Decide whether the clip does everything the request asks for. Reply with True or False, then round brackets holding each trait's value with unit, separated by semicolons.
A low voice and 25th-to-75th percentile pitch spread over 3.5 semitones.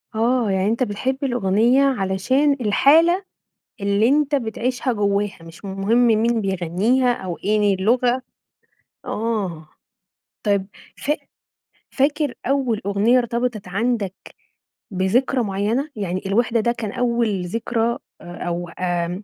False (220 Hz; 4.2 semitones)